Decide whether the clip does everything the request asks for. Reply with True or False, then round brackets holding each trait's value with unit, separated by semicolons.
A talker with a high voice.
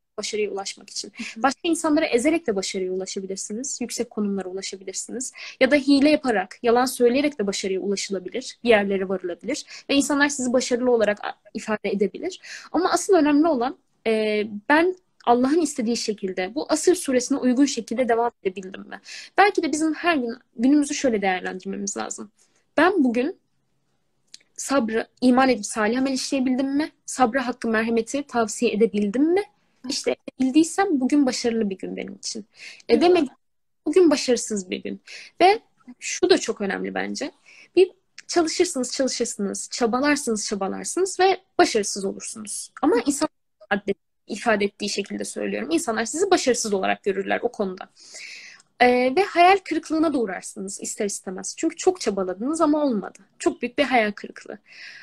True (245 Hz)